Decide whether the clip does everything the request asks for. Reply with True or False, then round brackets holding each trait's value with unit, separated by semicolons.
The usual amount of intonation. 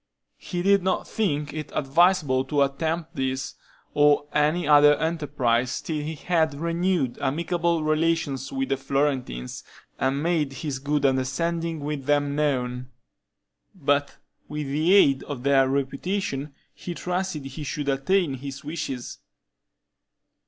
True (3.4 semitones)